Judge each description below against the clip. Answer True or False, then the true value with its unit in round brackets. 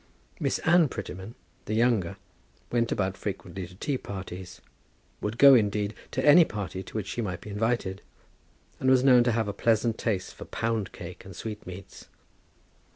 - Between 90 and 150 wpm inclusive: False (170 wpm)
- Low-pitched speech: True (105 Hz)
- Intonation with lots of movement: False (3.7 semitones)